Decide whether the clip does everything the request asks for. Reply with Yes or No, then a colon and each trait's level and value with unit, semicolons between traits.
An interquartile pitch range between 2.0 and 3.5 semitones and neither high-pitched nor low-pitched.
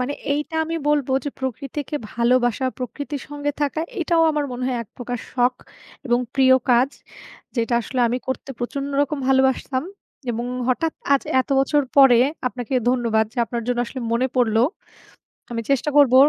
No: average, 2.8 semitones; very high, 260 Hz